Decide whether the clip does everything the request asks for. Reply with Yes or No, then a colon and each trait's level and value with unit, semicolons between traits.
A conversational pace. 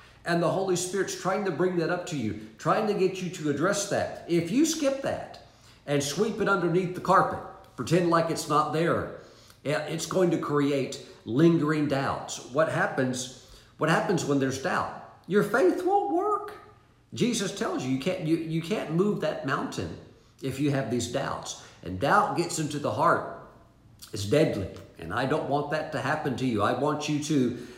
Yes: average, 190 wpm